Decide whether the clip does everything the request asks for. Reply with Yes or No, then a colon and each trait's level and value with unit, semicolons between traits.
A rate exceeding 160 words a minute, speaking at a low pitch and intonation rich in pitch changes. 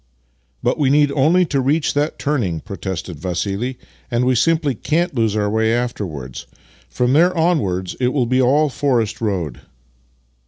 Yes: average, 180 wpm; low, 125 Hz; wide, 6.7 semitones